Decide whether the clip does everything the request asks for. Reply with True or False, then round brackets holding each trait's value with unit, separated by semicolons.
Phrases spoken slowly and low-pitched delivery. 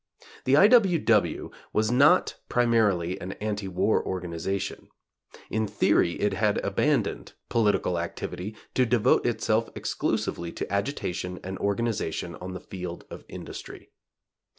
True (130 wpm; 100 Hz)